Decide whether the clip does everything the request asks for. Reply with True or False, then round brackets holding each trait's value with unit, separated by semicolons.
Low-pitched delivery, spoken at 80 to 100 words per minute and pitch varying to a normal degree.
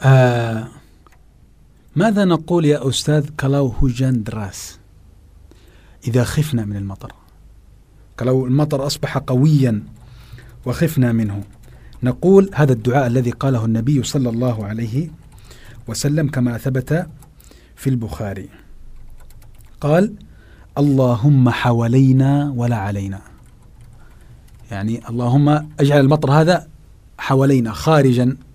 True (125 Hz; 90 wpm; 4.3 semitones)